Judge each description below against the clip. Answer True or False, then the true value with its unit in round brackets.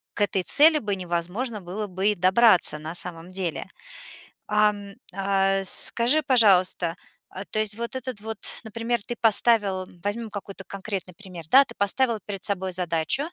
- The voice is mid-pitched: False (200 Hz)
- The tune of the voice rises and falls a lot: False (3.7 semitones)